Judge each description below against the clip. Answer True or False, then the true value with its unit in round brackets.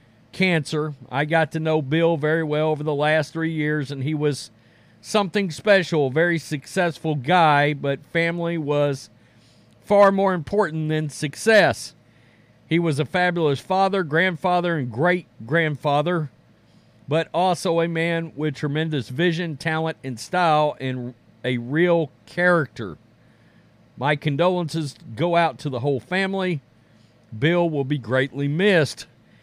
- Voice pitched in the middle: True (155 Hz)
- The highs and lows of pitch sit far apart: False (3.6 semitones)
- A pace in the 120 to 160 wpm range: True (135 wpm)